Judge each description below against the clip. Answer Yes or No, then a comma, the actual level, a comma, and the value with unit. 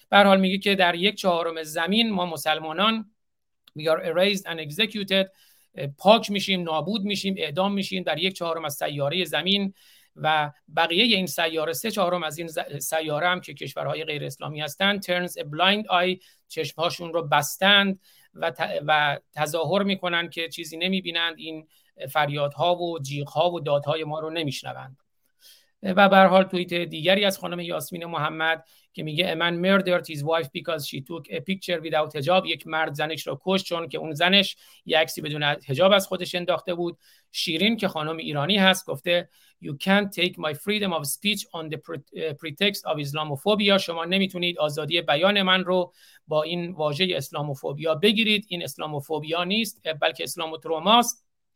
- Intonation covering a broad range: No, average, 3.4 semitones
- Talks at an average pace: No, fast, 160 wpm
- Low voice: No, medium, 170 Hz